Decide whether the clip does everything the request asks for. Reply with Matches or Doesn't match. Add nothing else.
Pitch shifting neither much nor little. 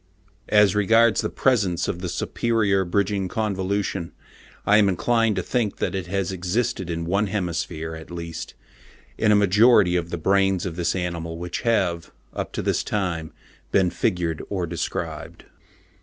Matches